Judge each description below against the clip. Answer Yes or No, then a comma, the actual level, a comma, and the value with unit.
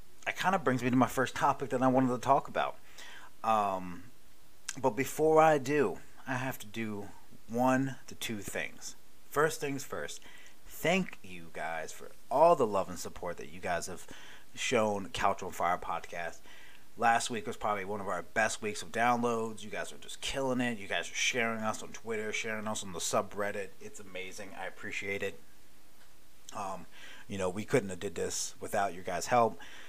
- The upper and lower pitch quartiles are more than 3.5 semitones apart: Yes, average, 3.9 semitones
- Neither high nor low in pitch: No, low, 120 Hz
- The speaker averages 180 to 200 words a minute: Yes, average, 190 wpm